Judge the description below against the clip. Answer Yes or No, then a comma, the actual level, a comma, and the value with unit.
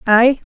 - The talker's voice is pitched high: Yes, high, 240 Hz